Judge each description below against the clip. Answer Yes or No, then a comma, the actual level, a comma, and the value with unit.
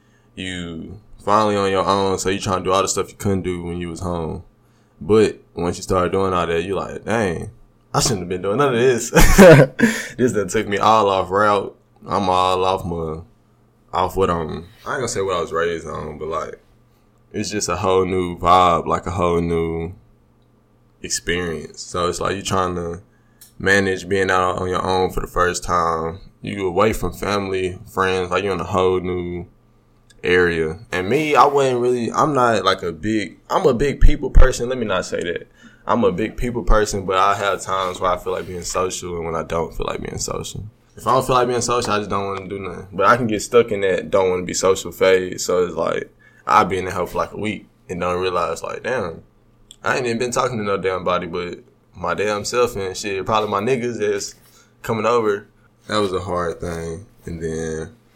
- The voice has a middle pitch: No, very low, 95 Hz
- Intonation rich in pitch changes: No, average, 3.3 semitones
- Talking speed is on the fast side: Yes, fast, 225 wpm